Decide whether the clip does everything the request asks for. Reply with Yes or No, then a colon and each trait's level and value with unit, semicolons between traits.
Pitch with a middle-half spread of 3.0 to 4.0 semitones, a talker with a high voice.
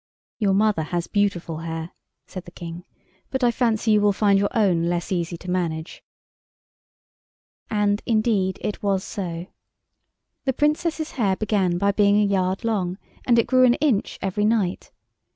Yes: average, 3.5 semitones; high, 200 Hz